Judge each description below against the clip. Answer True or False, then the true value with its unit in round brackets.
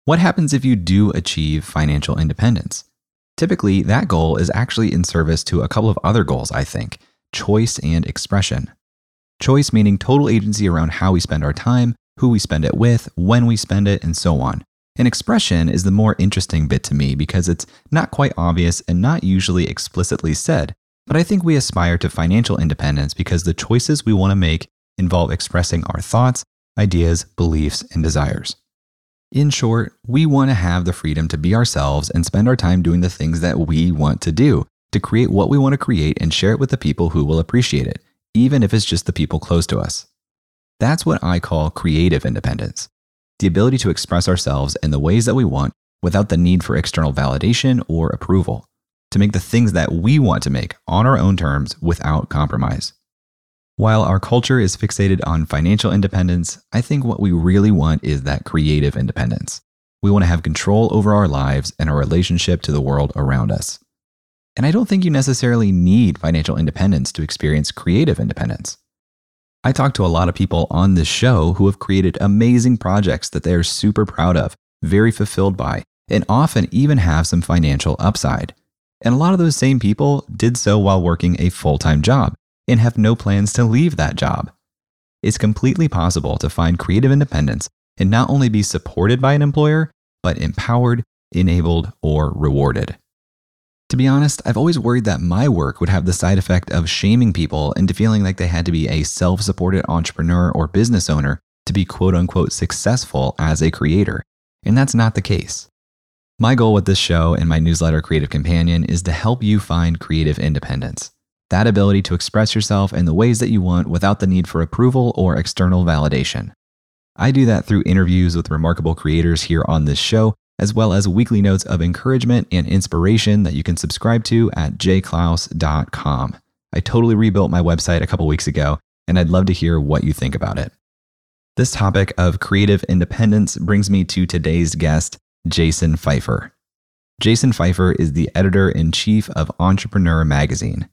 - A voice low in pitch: True (90 Hz)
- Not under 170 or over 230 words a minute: True (190 wpm)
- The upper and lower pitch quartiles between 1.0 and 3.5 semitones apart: False (5.2 semitones)